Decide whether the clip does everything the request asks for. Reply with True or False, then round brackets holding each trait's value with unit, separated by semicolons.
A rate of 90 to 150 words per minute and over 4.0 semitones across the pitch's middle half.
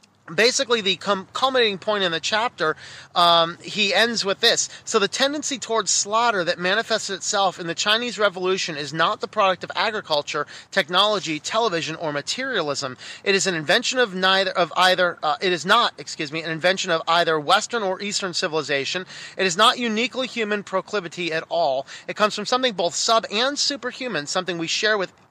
False (185 wpm; 4.6 semitones)